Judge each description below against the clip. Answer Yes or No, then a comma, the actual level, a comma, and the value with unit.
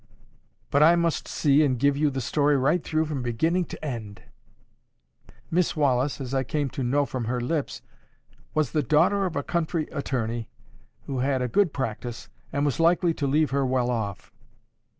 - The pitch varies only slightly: No, average, 3.7 semitones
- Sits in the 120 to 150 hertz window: Yes, medium, 140 Hz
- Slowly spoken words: No, average, 180 wpm